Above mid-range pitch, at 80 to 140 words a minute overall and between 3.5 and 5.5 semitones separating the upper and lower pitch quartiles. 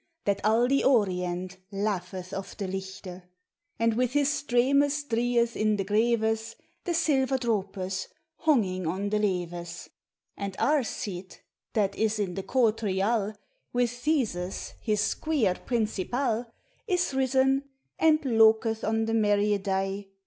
Yes: high, 220 Hz; slow, 135 wpm; average, 4.2 semitones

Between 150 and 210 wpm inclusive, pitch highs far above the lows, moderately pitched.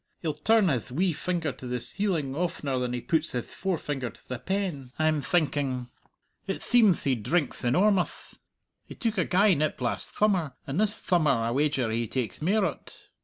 Yes: average, 180 wpm; wide, 6.4 semitones; medium, 155 Hz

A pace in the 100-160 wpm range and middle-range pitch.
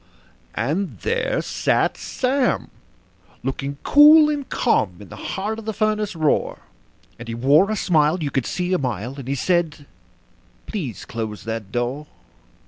Yes: average, 150 wpm; medium, 155 Hz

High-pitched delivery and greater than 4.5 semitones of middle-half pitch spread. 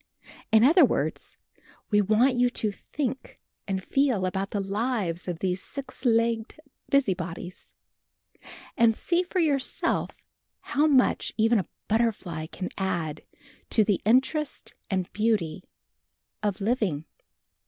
Yes: high, 215 Hz; average, 5.2 semitones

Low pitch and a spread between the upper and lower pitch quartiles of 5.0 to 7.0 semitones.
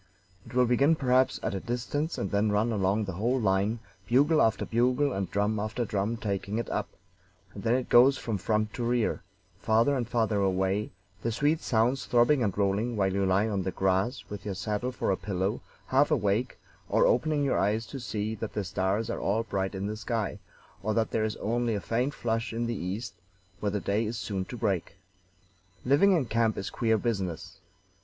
No: low, 110 Hz; average, 3.3 semitones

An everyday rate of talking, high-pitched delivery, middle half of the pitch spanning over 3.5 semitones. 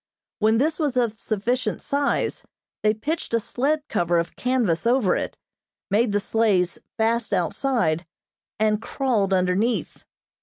No: slow, 130 wpm; high, 225 Hz; average, 4.4 semitones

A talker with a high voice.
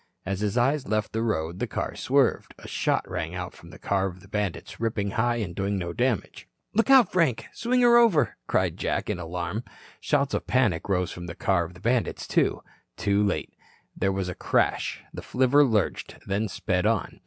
No: low, 105 Hz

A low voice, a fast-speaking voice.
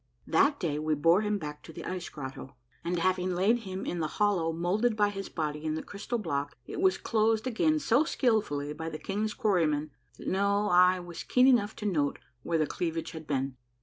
No: medium, 180 Hz; fast, 210 wpm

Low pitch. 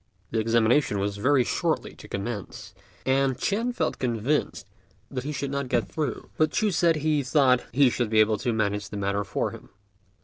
Yes: low, 125 Hz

